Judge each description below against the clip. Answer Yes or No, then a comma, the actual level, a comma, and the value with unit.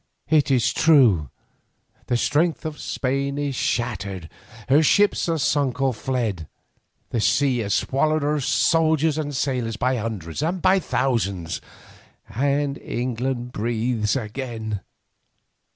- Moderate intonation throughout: Yes, average, 4.2 semitones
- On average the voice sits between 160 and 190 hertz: No, low, 130 Hz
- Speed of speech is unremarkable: No, slow, 125 wpm